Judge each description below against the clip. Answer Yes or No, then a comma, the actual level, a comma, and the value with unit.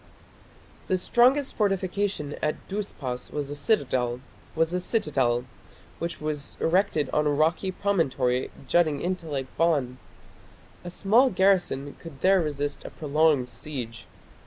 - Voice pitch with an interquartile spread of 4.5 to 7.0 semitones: Yes, average, 5.1 semitones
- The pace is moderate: No, slow, 115 wpm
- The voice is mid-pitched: Yes, medium, 155 Hz